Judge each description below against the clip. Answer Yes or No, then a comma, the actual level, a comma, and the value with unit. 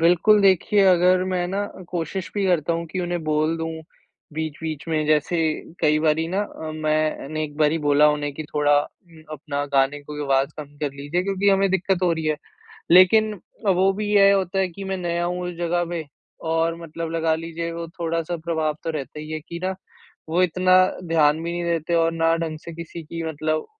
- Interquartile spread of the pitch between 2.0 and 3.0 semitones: Yes, narrow, 2.6 semitones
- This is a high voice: No, medium, 165 Hz